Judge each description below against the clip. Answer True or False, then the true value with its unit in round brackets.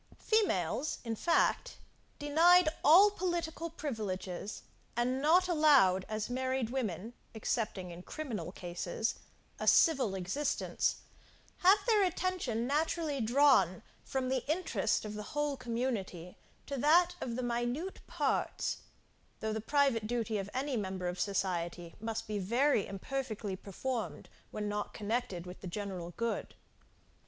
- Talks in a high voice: True (235 Hz)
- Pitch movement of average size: False (6.7 semitones)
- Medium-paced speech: False (130 wpm)